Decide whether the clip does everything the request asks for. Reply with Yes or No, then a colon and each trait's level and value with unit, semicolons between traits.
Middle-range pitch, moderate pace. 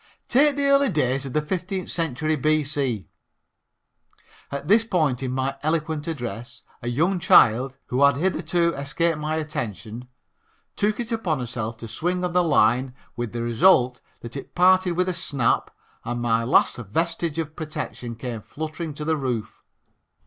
Yes: medium, 150 Hz; average, 165 wpm